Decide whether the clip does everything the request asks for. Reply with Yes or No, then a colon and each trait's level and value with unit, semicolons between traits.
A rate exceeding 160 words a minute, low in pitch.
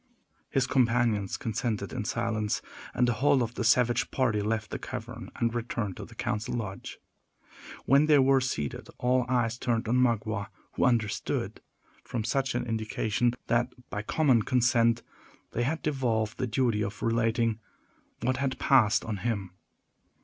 No: average, 155 wpm; low, 115 Hz